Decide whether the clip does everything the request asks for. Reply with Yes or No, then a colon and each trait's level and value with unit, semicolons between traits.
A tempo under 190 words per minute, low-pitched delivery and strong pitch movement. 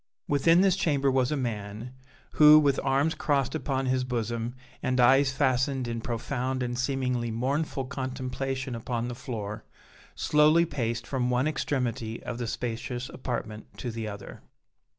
No: average, 150 wpm; low, 130 Hz; average, 2.7 semitones